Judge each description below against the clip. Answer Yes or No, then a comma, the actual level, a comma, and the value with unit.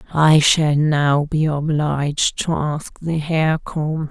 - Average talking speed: Yes, average, 145 wpm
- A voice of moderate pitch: Yes, medium, 150 Hz